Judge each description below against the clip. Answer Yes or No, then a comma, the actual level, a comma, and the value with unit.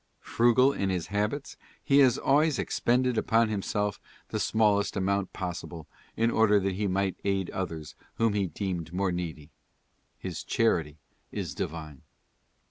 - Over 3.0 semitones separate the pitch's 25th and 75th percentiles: Yes, average, 4.1 semitones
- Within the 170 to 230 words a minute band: No, average, 140 wpm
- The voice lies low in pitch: Yes, low, 100 Hz